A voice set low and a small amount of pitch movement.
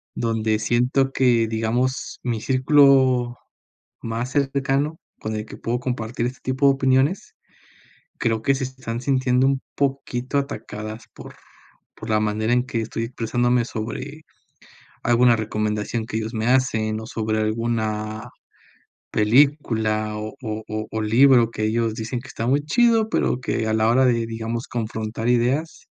No: low, 120 Hz; average, 3.0 semitones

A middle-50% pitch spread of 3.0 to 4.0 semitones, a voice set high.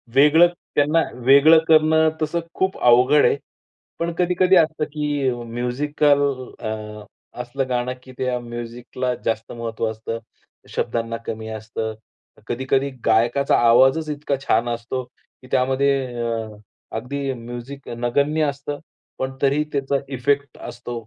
No: average, 3.6 semitones; low, 130 Hz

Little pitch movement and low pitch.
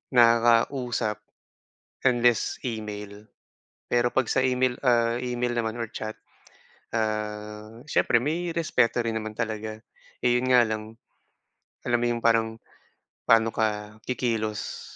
Yes: narrow, 2.0 semitones; low, 115 Hz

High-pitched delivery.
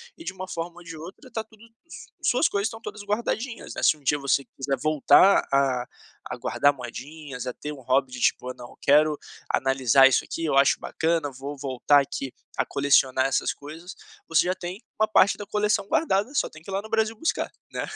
No: medium, 155 Hz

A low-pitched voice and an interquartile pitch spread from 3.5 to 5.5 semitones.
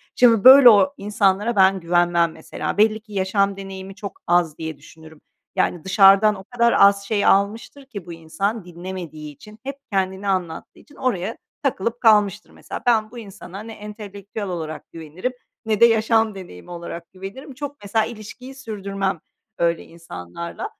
No: high, 200 Hz; average, 4.0 semitones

